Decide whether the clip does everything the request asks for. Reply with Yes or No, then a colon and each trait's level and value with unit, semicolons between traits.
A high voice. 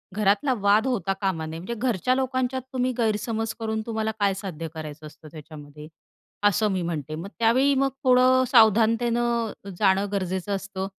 Yes: high, 210 Hz